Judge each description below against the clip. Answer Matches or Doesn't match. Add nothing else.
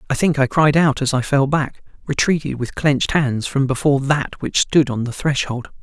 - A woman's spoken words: Doesn't match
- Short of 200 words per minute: Doesn't match